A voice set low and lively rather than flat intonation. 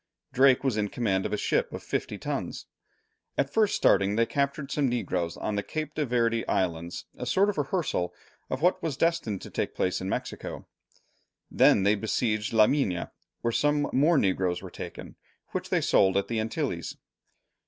Yes: low, 115 Hz; wide, 6.3 semitones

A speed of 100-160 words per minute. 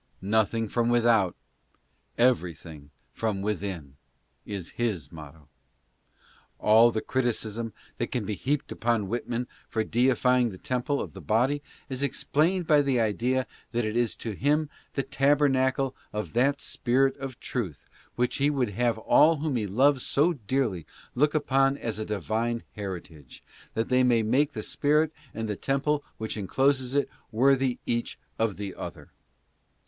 Yes: average, 155 wpm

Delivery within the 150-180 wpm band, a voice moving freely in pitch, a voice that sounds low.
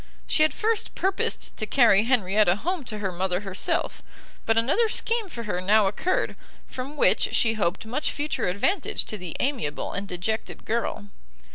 No: average, 165 wpm; wide, 7.0 semitones; high, 220 Hz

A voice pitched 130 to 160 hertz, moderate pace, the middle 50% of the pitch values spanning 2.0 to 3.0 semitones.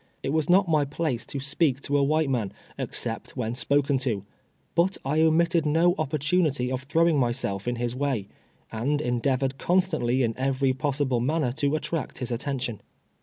No: medium, 140 Hz; average, 170 wpm; average, 3.8 semitones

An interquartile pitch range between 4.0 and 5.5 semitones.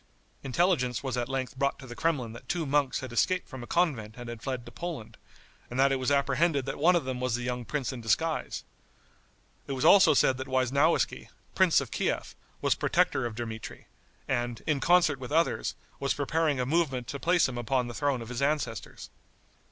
No: average, 3.5 semitones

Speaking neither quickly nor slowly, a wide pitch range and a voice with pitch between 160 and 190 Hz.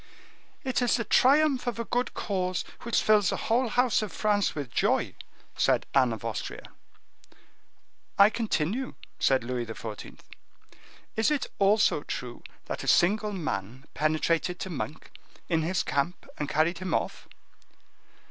Yes: average, 145 wpm; wide, 7.5 semitones; medium, 185 Hz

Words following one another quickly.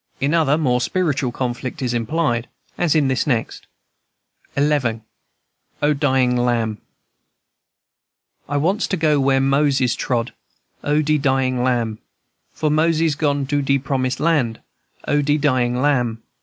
No: average, 140 wpm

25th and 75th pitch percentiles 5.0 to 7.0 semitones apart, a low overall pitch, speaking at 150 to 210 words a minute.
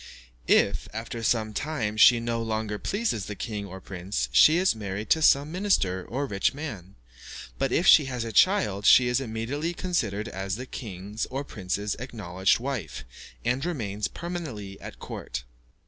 Yes: wide, 5.6 semitones; low, 115 Hz; average, 165 wpm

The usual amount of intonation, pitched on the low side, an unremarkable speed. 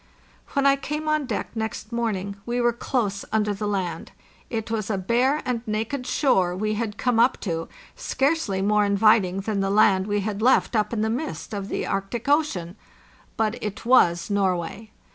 No: average, 3.3 semitones; high, 215 Hz; average, 180 wpm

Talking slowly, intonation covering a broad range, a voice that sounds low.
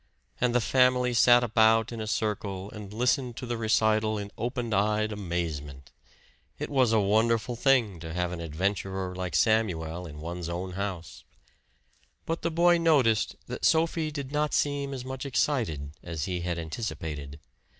No: average, 160 wpm; wide, 5.9 semitones; low, 110 Hz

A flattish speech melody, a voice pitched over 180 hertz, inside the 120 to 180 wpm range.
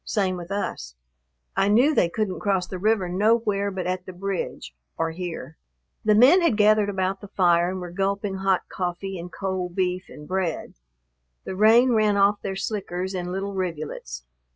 Yes: narrow, 2.3 semitones; high, 190 Hz; average, 175 wpm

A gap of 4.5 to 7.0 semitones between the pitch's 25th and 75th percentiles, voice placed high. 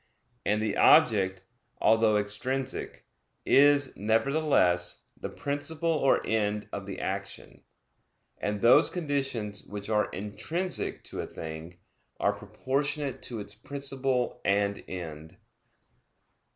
No: wide, 5.4 semitones; low, 110 Hz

